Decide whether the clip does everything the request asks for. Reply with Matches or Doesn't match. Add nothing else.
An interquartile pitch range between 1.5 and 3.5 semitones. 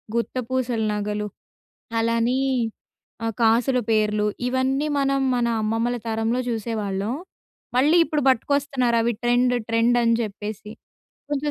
Matches